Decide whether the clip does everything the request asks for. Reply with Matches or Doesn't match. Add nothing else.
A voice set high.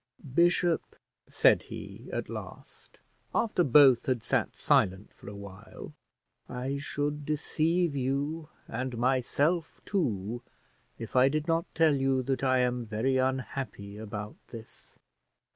Doesn't match